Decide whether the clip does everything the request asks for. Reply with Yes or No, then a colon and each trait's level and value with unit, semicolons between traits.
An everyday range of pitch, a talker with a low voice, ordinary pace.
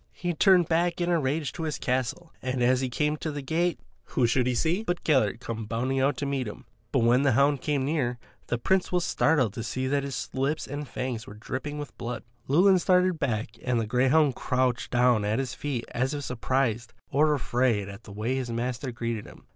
No: average, 3.8 semitones; low, 130 Hz; fast, 225 wpm